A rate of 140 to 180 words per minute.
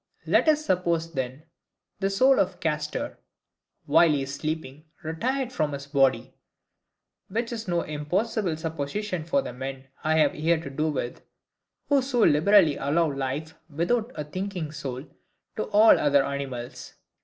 Yes: average, 150 wpm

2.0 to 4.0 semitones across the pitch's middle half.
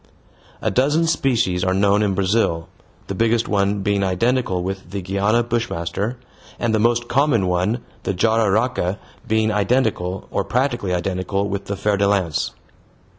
Yes: average, 3.5 semitones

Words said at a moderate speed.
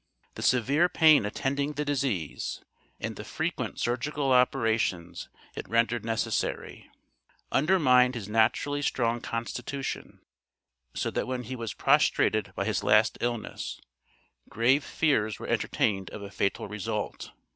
No: slow, 125 wpm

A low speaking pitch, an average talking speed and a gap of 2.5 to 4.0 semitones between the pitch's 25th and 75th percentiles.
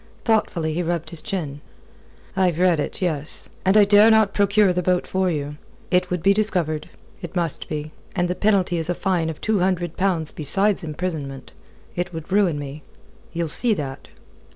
No: medium, 175 Hz; average, 180 wpm; average, 3.5 semitones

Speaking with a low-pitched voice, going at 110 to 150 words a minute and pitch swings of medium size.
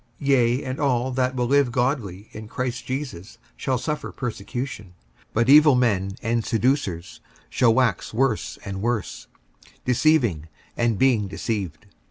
Yes: low, 120 Hz; average, 145 wpm; average, 3.7 semitones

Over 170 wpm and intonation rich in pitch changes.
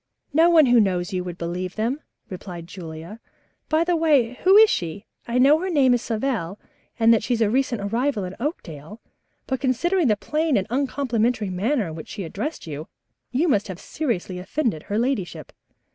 Yes: average, 185 wpm; wide, 7.1 semitones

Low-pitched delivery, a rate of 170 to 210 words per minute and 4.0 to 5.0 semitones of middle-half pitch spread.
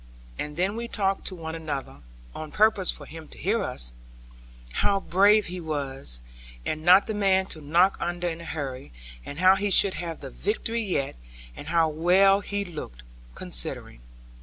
No: medium, 175 Hz; average, 175 wpm; average, 4.5 semitones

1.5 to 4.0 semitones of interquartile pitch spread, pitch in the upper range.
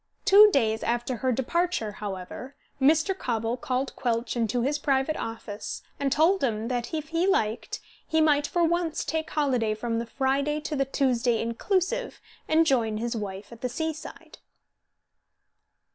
No: wide, 5.4 semitones; very high, 265 Hz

